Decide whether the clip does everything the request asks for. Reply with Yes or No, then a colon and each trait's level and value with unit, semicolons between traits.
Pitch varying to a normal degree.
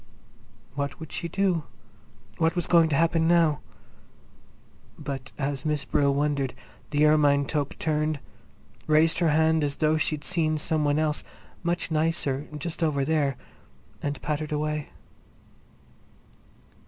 No: narrow, 1.9 semitones